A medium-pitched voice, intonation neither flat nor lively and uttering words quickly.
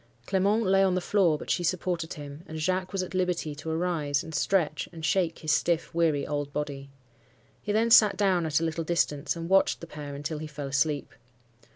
Yes: medium, 165 Hz; average, 3.7 semitones; fast, 210 wpm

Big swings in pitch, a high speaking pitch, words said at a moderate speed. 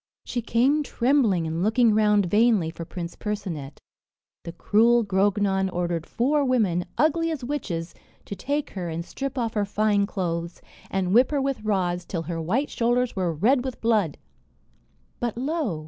Yes: wide, 5.9 semitones; high, 210 Hz; average, 160 wpm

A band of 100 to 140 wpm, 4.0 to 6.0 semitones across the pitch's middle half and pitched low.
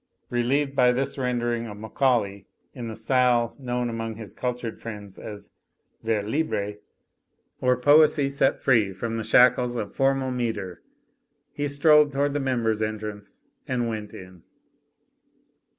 No: slow, 135 wpm; average, 3.4 semitones; low, 120 Hz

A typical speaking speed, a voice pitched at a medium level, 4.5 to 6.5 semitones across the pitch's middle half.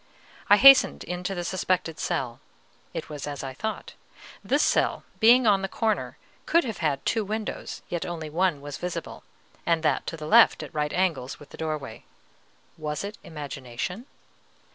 Yes: average, 165 wpm; medium, 165 Hz; average, 5.1 semitones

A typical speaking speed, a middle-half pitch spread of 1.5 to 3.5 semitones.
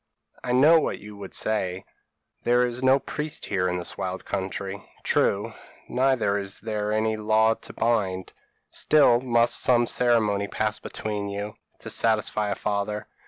Yes: average, 160 wpm; average, 3.0 semitones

